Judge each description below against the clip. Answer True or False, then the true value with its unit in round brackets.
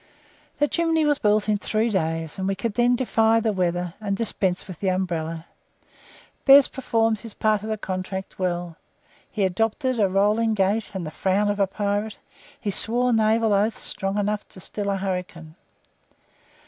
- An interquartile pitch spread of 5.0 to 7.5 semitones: False (3.1 semitones)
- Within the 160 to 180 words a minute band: True (175 wpm)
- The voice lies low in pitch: False (205 Hz)